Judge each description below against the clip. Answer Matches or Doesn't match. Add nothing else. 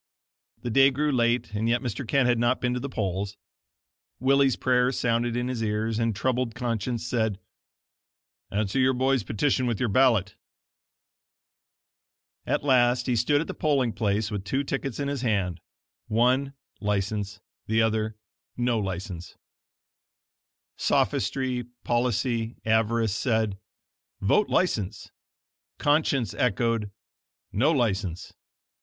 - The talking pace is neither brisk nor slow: Doesn't match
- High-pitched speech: Doesn't match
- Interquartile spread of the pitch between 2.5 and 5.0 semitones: Matches